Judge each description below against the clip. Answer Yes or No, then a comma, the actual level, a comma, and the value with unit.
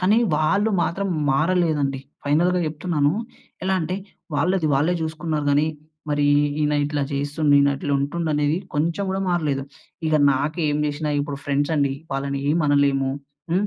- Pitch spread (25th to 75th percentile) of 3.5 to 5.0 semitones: No, average, 2.9 semitones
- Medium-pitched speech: Yes, medium, 150 Hz